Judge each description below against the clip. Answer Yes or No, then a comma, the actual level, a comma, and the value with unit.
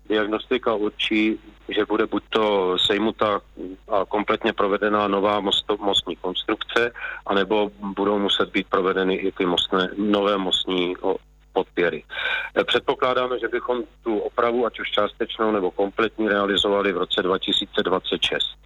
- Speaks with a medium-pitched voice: No, low, 105 Hz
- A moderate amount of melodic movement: No, narrow, 1.9 semitones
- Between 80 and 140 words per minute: Yes, average, 120 wpm